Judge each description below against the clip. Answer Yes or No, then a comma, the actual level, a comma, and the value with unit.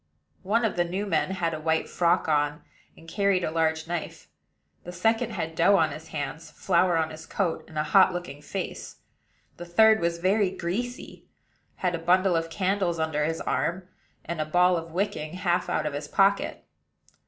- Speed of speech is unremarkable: Yes, average, 190 wpm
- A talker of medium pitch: Yes, medium, 175 Hz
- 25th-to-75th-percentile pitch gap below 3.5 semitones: Yes, average, 2.8 semitones